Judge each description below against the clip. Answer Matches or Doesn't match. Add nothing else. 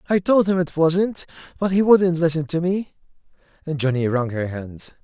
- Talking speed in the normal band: Matches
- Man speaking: Matches